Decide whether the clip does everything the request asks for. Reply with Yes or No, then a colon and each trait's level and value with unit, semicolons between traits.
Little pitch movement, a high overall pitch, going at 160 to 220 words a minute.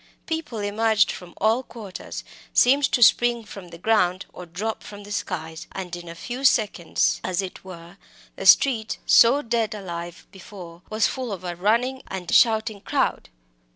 No: average, 4.5 semitones; high, 205 Hz; average, 165 wpm